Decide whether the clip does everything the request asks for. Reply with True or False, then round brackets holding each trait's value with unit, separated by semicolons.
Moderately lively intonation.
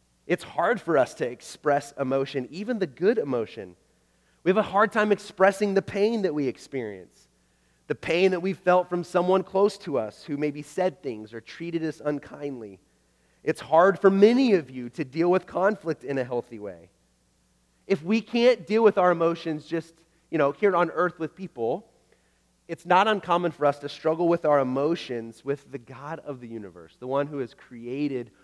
False (6.1 semitones)